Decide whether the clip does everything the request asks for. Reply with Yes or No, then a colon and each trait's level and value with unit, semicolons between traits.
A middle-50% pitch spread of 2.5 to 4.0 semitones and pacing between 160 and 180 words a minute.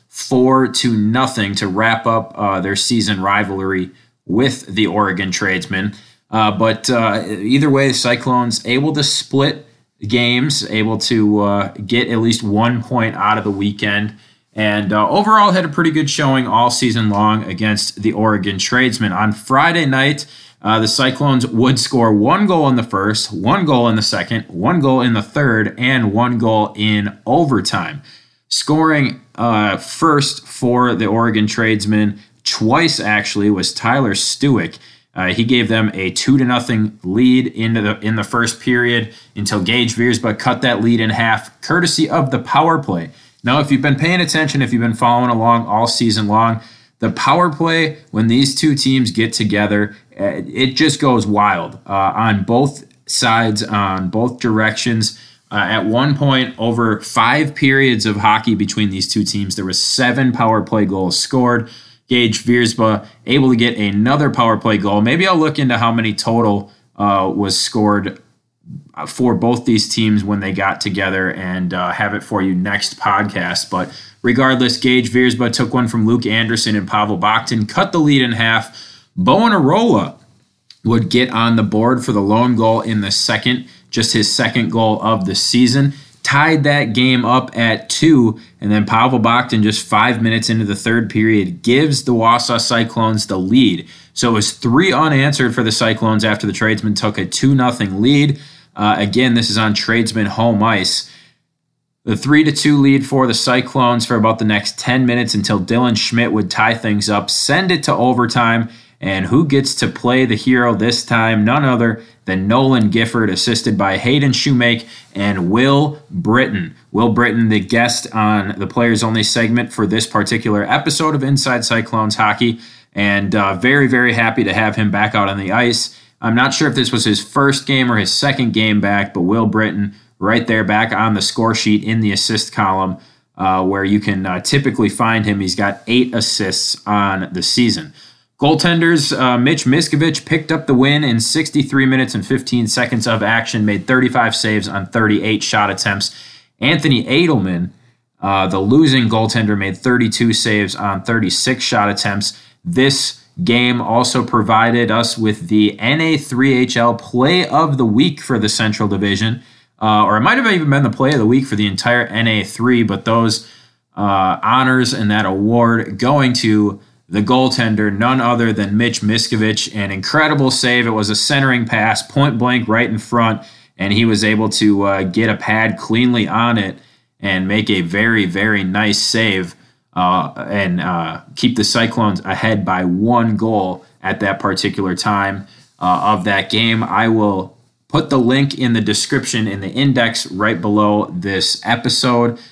Yes: average, 3.0 semitones; average, 175 wpm